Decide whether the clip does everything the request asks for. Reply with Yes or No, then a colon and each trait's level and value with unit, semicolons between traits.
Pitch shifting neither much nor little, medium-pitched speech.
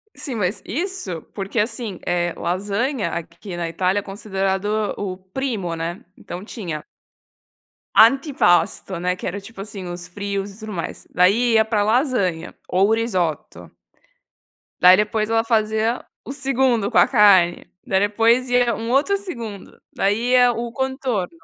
No: average, 4.4 semitones; high, 210 Hz